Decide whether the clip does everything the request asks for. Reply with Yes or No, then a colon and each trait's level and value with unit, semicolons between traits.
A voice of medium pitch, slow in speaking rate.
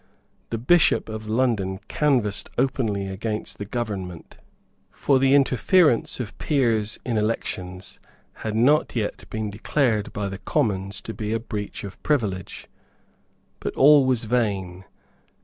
No: low, 110 Hz; slow, 130 wpm